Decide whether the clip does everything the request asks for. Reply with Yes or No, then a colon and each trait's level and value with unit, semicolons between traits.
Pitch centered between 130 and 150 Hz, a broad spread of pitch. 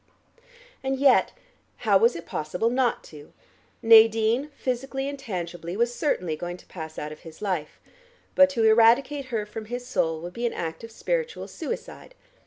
No: high, 225 Hz; wide, 6.8 semitones